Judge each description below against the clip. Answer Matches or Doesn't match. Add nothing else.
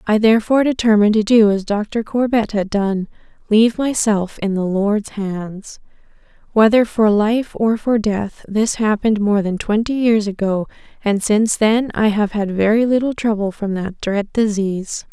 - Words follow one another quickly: Doesn't match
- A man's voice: Doesn't match